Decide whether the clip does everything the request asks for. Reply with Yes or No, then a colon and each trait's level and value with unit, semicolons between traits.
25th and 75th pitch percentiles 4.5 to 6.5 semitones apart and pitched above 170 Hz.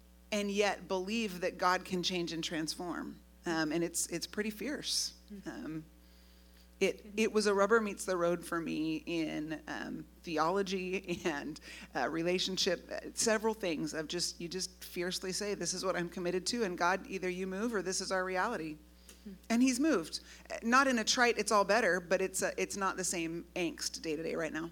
No: average, 3.7 semitones; medium, 185 Hz